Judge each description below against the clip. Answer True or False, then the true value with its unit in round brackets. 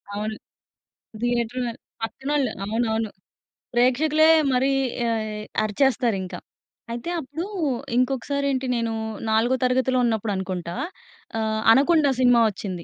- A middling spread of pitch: True (3.5 semitones)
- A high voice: True (240 Hz)